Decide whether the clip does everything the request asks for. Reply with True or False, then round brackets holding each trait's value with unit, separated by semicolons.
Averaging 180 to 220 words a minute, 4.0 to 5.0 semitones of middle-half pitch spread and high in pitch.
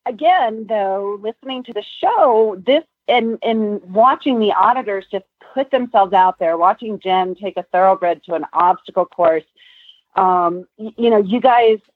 False (160 wpm; 4.5 semitones; 210 Hz)